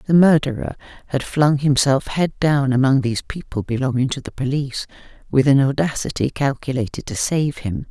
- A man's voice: No, female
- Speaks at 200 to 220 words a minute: No, average, 160 wpm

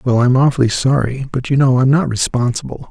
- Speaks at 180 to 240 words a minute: Yes, fast, 205 wpm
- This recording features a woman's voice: No, male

